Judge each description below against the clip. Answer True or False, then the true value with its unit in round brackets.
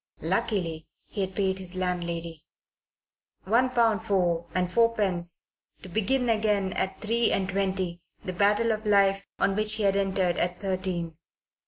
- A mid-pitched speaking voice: False (195 Hz)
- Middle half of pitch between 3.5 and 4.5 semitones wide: False (2.9 semitones)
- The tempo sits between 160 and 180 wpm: False (150 wpm)